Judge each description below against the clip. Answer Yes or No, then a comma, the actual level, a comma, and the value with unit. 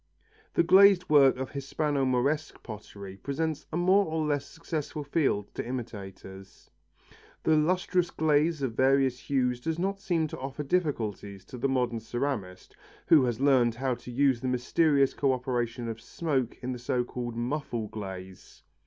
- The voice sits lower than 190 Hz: Yes, low, 135 Hz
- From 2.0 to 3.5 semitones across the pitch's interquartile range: No, average, 4.3 semitones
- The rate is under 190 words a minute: Yes, average, 160 wpm